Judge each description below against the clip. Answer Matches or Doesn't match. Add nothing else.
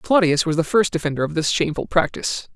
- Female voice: Doesn't match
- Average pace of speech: Doesn't match